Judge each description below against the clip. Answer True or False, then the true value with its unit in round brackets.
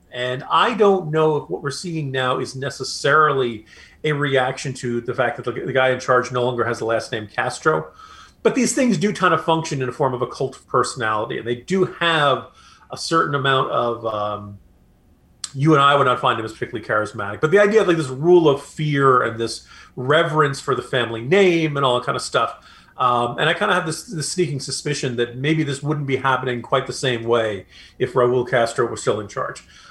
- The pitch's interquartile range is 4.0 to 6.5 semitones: True (4.4 semitones)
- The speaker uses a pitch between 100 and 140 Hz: True (135 Hz)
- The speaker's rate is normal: False (225 wpm)